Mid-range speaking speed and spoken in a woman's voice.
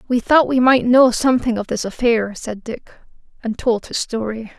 Yes: average, 195 wpm; female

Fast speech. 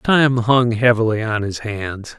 No: average, 165 wpm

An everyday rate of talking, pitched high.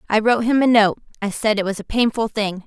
No: fast, 270 wpm; high, 220 Hz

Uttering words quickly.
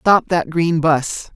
No: average, 175 wpm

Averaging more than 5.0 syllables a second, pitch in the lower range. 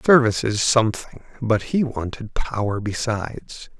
No: 4.7 syllables/s; low, 115 Hz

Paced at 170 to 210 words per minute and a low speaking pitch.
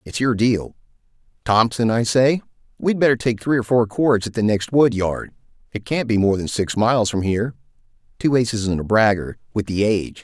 Yes: average, 180 wpm; low, 110 Hz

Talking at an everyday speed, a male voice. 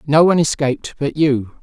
Yes: average, 185 wpm; male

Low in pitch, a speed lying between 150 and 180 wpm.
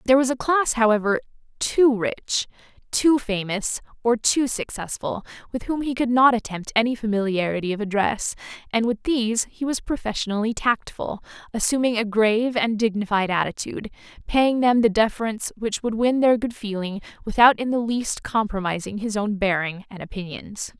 No: high, 225 Hz; average, 160 wpm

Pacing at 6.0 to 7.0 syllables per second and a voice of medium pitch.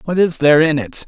Yes: 6.5 syllables/s; medium, 160 Hz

